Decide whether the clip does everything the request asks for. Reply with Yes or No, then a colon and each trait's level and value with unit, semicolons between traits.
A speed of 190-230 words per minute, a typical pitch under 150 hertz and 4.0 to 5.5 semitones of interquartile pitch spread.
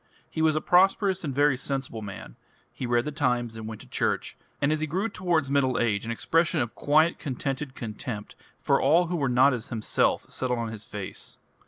Yes: fast, 205 wpm; low, 135 Hz; average, 5.0 semitones